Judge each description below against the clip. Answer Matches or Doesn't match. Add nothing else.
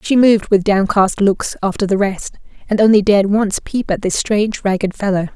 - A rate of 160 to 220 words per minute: Matches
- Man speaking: Doesn't match